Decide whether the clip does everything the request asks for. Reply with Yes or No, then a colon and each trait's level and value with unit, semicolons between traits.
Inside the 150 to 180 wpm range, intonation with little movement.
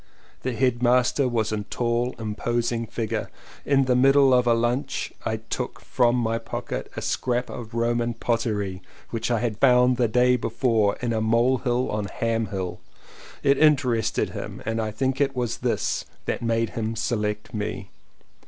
Yes: average, 160 wpm; narrow, 2.0 semitones